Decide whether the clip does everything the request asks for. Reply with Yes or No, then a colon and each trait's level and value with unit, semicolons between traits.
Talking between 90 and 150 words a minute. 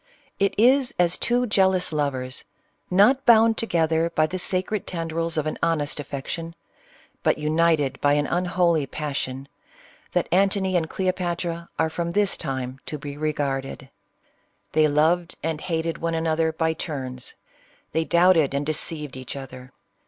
Yes: average, 145 wpm